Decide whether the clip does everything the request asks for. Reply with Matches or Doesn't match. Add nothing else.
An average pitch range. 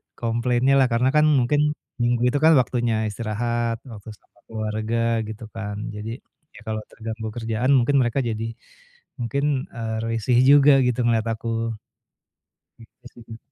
Doesn't match